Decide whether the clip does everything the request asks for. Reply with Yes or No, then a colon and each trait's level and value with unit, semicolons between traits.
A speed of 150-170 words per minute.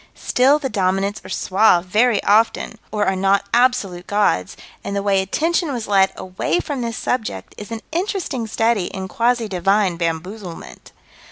Yes: average, 160 wpm